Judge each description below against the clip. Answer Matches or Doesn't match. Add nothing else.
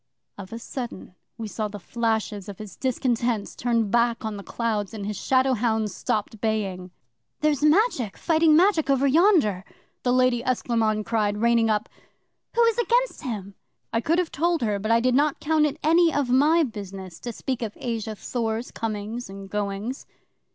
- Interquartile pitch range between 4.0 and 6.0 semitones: Matches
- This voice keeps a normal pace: Matches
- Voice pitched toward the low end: Doesn't match